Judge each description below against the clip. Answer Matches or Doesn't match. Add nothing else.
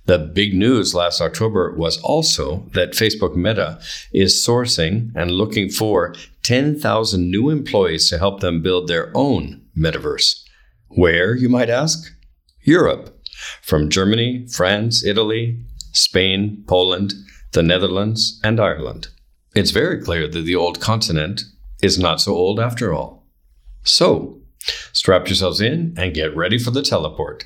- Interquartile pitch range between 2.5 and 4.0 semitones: Doesn't match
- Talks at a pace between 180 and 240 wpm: Doesn't match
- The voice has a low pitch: Matches